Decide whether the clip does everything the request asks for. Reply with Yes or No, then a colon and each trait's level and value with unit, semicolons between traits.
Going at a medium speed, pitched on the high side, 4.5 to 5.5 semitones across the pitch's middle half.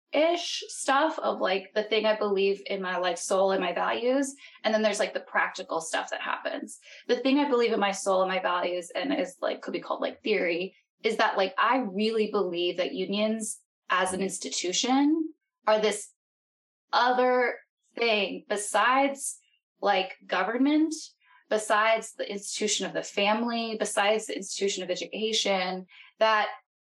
Yes: average, 160 wpm; high, 215 Hz; average, 5.0 semitones